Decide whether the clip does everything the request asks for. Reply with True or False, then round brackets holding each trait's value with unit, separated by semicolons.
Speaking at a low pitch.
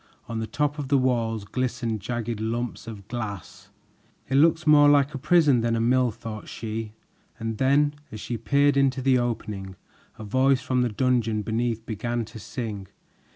True (120 Hz)